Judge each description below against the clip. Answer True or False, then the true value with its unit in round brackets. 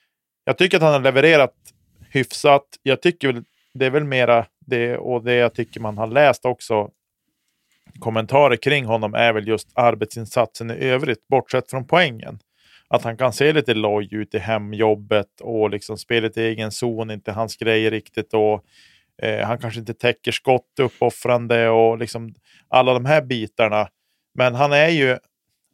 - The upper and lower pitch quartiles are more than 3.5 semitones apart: False (2.7 semitones)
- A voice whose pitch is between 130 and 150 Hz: False (115 Hz)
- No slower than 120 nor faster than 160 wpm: False (170 wpm)